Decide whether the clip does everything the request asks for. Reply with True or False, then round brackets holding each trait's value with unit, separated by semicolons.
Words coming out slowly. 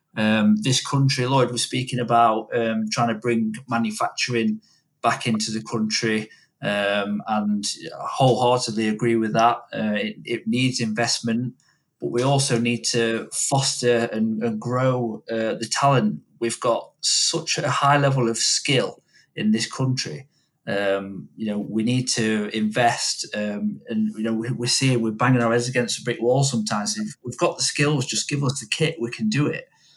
False (175 wpm)